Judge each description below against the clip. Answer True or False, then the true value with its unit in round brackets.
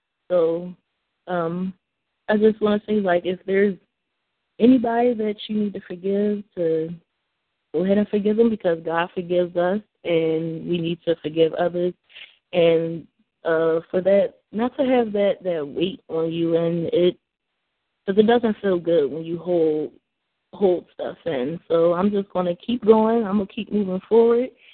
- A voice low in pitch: False (185 Hz)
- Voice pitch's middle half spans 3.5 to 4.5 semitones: True (3.9 semitones)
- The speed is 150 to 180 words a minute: True (165 wpm)